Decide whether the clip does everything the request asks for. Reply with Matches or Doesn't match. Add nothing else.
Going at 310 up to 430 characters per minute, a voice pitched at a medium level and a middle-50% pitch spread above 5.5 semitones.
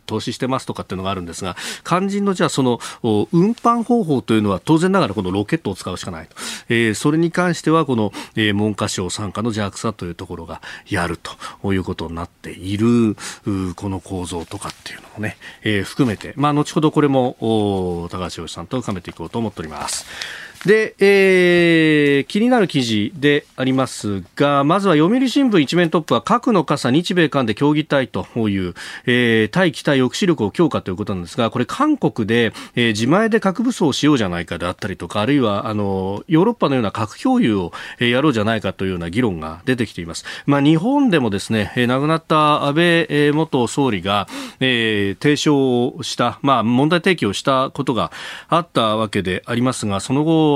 Doesn't match